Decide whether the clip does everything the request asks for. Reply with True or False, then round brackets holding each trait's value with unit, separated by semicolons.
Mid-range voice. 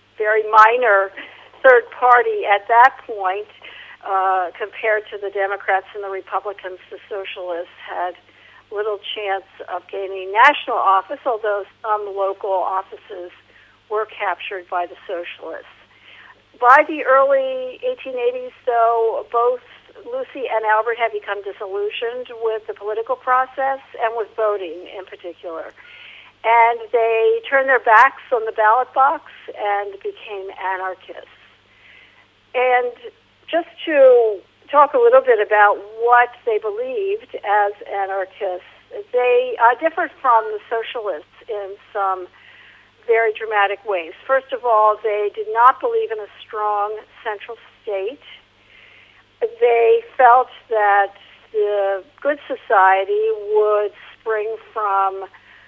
False (220 Hz)